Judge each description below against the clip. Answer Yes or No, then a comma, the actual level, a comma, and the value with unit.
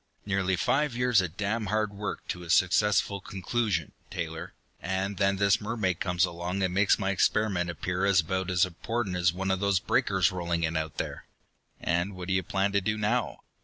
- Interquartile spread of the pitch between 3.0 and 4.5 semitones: No, narrow, 2.5 semitones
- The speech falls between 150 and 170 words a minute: No, average, 190 wpm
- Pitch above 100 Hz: No, very low, 95 Hz